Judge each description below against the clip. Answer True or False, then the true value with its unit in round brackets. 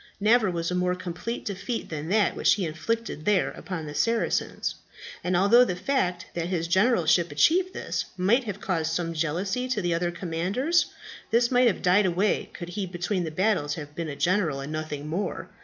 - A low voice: False (180 Hz)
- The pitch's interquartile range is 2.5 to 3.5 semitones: False (4.2 semitones)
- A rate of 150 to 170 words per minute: False (190 wpm)